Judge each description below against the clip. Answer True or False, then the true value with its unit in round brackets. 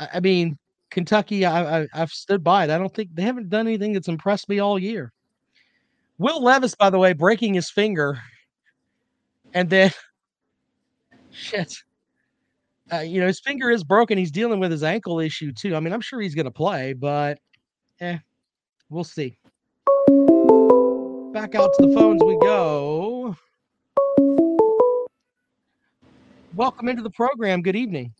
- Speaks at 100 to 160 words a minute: True (150 wpm)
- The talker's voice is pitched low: False (200 Hz)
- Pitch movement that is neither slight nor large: False (6.9 semitones)